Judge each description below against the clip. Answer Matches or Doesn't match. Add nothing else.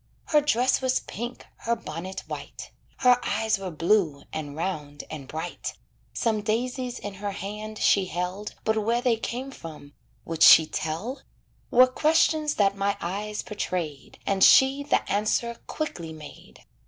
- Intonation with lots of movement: Matches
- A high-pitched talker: Matches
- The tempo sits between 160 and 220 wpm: Doesn't match